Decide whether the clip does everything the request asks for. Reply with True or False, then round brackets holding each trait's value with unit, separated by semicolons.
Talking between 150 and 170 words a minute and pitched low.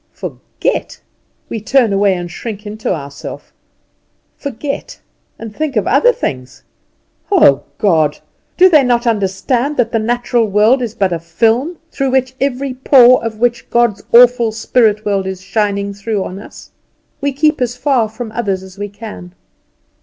False (155 wpm; 225 Hz)